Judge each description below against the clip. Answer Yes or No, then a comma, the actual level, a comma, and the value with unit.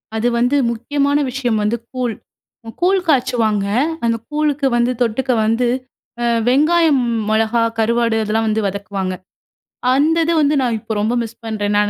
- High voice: Yes, high, 235 Hz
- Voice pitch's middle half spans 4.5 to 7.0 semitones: No, average, 3.9 semitones